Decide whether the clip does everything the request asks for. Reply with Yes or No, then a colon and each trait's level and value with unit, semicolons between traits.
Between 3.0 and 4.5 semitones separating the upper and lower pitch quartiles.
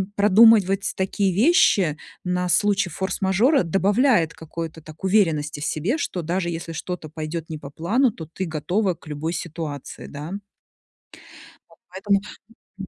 Yes: average, 3.7 semitones